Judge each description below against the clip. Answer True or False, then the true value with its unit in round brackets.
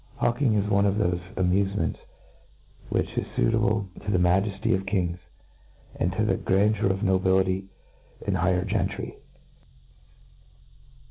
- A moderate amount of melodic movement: False (1.7 semitones)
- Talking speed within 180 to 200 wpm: False (135 wpm)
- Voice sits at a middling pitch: False (95 Hz)